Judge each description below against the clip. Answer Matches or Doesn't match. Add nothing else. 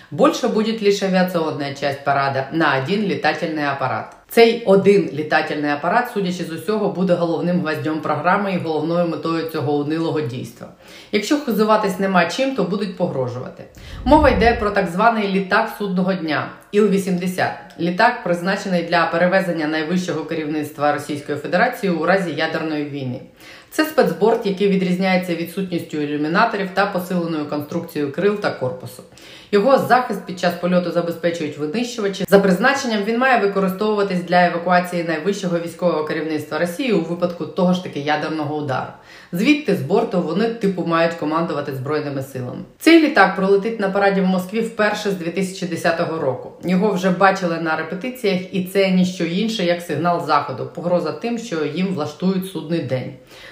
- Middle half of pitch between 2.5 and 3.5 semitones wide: Doesn't match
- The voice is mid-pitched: Matches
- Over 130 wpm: Matches